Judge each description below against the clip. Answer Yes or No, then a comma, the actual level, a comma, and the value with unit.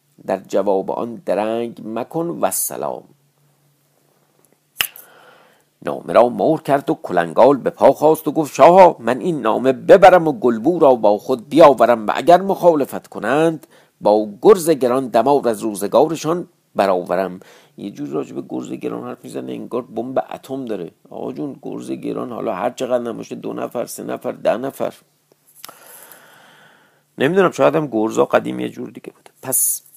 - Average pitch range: No, wide, 6.0 semitones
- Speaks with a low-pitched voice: Yes, low, 130 Hz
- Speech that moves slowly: No, average, 150 wpm